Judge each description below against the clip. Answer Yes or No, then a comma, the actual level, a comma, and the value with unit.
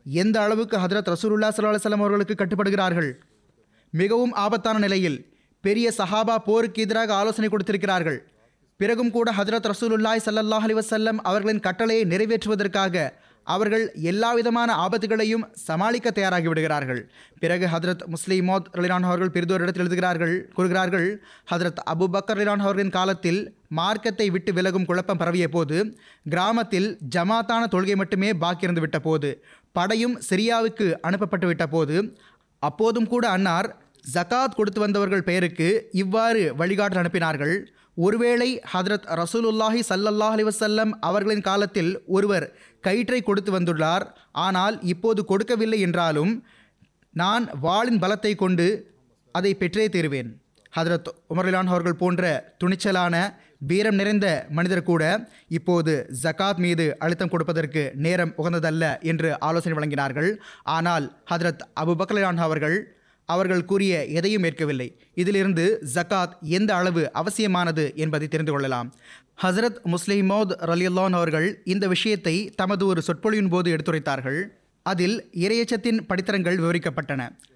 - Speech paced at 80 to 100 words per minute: No, average, 110 wpm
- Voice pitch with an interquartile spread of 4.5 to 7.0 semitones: No, average, 3.9 semitones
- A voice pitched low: No, medium, 185 Hz